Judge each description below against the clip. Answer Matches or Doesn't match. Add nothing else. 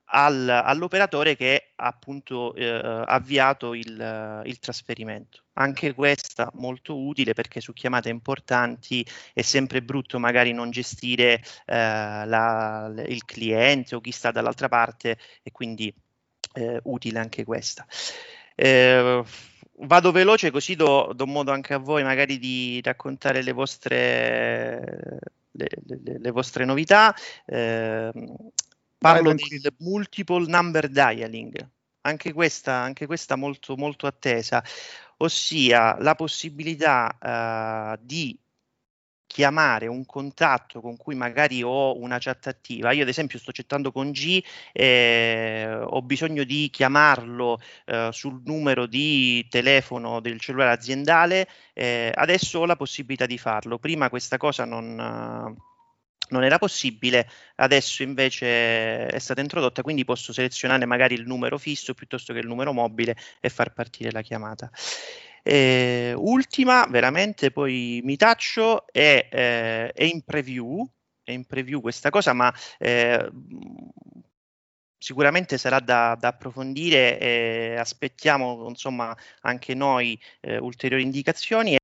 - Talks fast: Doesn't match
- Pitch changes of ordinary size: Matches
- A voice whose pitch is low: Matches